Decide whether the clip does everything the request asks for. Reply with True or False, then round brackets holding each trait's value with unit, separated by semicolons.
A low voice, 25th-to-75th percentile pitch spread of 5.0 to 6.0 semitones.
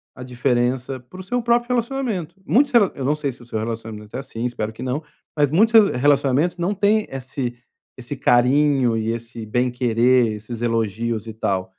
True (125 Hz; 5.3 semitones)